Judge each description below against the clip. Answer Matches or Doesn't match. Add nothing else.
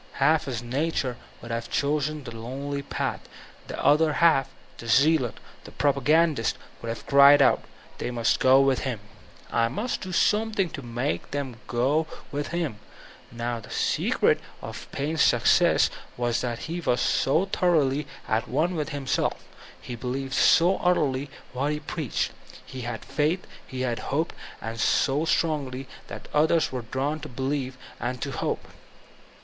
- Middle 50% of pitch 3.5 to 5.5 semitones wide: Matches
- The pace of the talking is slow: Doesn't match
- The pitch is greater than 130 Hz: Matches